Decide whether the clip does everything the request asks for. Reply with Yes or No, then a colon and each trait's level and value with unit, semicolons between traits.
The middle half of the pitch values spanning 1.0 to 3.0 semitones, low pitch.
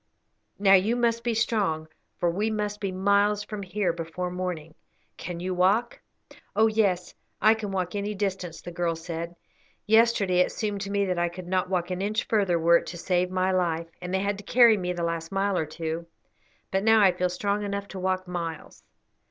No: average, 2.7 semitones; medium, 185 Hz